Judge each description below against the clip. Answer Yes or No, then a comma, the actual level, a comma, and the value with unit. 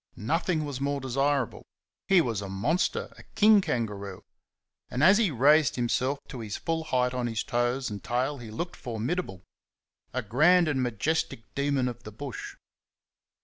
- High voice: No, low, 130 Hz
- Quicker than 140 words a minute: Yes, average, 160 wpm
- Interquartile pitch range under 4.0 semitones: No, average, 4.8 semitones